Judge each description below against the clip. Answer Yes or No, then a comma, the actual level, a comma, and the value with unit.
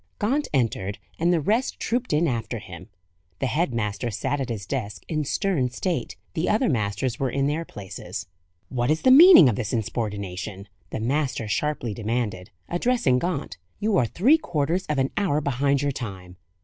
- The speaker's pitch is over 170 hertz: No, low, 135 Hz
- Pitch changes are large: Yes, wide, 7.0 semitones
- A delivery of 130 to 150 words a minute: No, average, 175 wpm